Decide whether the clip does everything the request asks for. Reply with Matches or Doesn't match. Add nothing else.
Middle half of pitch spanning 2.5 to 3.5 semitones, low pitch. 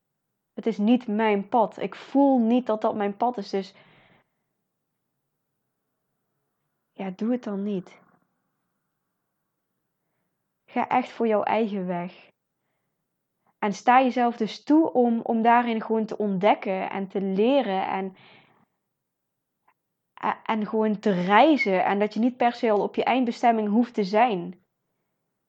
Doesn't match